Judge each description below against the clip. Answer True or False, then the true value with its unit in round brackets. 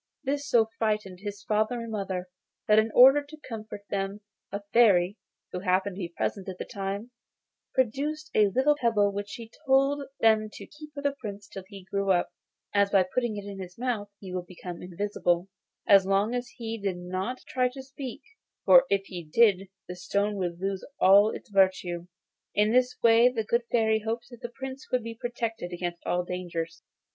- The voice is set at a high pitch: True (210 Hz)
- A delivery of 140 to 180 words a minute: False (190 wpm)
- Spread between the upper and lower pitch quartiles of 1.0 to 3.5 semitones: False (4.0 semitones)